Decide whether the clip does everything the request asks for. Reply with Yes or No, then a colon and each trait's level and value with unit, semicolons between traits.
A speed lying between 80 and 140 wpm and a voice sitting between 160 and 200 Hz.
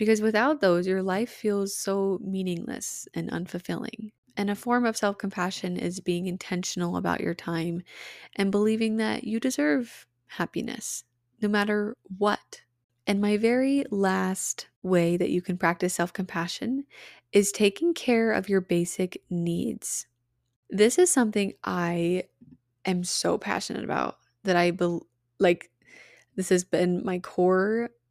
Yes: slow, 135 wpm; high, 190 Hz